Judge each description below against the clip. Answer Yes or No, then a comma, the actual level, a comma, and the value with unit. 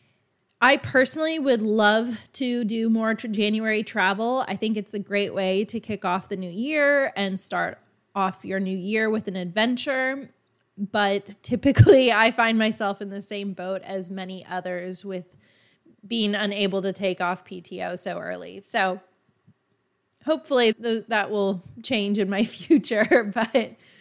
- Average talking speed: Yes, average, 155 wpm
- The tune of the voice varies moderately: Yes, average, 3.1 semitones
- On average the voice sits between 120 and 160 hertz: No, high, 205 Hz